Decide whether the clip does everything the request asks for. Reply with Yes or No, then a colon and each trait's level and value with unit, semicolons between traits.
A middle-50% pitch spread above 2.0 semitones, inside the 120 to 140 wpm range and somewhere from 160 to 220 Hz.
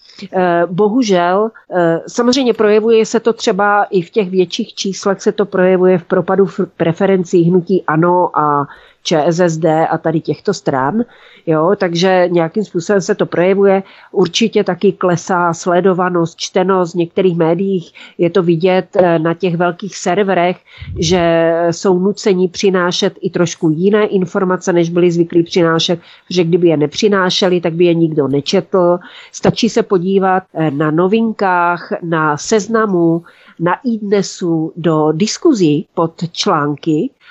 Yes: average, 2.7 semitones; average, 130 wpm; medium, 185 Hz